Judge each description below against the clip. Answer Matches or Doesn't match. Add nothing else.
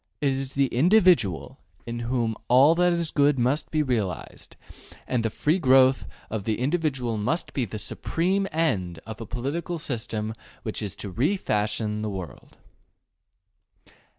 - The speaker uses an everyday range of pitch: Doesn't match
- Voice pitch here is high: Doesn't match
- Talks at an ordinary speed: Matches